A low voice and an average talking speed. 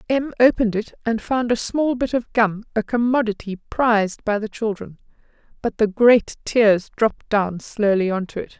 No: high, 220 Hz; average, 180 wpm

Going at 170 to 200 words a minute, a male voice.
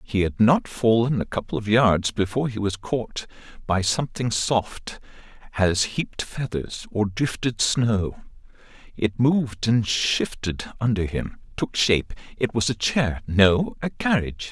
No: average, 145 wpm; male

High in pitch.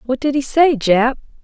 Yes: very high, 265 Hz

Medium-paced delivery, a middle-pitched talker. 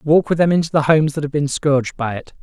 No: fast, 295 wpm; medium, 150 Hz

